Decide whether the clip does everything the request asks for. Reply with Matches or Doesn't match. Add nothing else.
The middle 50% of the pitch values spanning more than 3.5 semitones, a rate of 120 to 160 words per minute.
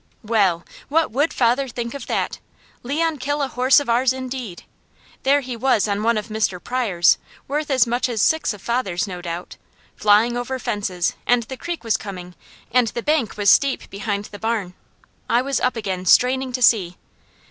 Doesn't match